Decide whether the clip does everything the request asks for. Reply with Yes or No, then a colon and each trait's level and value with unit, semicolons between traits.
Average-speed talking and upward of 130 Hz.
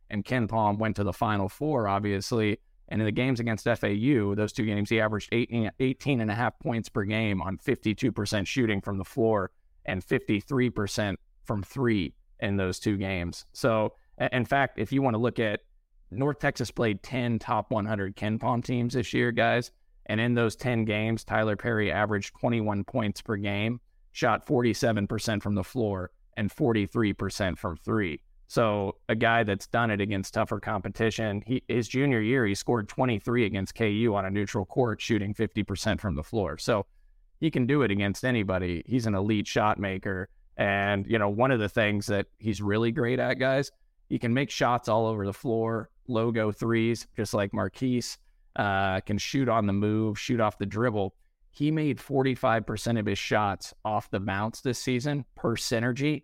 No: average, 180 wpm; low, 110 Hz